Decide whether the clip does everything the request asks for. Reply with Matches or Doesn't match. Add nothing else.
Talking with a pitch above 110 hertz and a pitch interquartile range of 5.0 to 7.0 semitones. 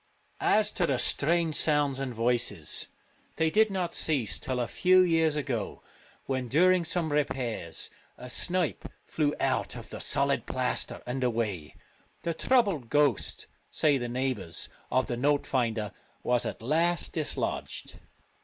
Matches